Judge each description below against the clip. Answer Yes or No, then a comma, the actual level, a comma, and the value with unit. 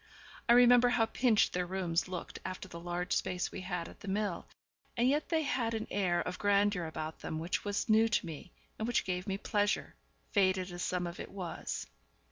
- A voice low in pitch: No, high, 190 Hz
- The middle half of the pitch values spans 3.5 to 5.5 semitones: Yes, average, 3.8 semitones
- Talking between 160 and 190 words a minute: No, fast, 205 wpm